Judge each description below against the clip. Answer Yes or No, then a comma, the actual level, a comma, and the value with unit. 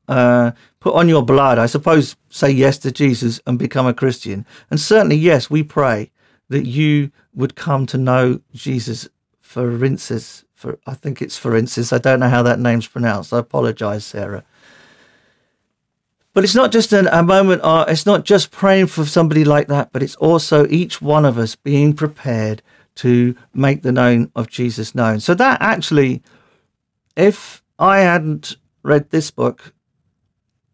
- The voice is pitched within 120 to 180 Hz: Yes, low, 135 Hz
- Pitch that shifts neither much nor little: Yes, average, 4.3 semitones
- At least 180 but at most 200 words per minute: No, average, 170 wpm